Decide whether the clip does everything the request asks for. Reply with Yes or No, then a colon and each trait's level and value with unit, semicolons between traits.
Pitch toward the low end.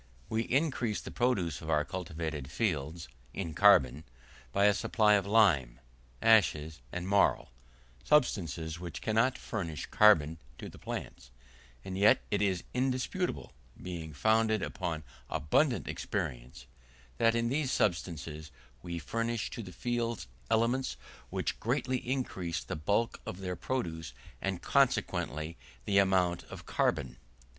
Yes: very low, 95 Hz